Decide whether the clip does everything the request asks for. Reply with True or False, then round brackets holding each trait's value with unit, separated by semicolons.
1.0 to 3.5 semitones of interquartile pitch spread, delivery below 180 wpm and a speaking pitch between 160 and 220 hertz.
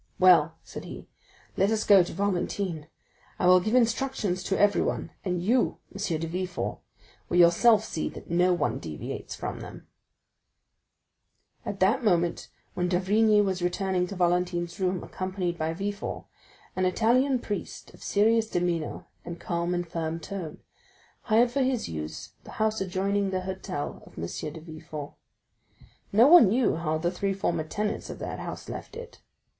True (3.2 semitones; 160 wpm; 185 Hz)